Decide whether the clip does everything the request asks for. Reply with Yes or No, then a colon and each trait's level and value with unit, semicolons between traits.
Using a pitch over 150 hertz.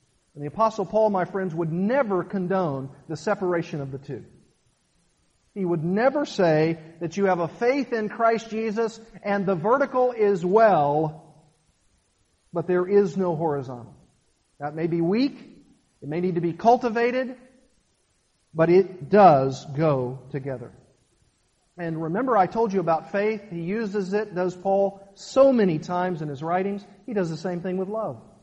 Yes: medium, 185 Hz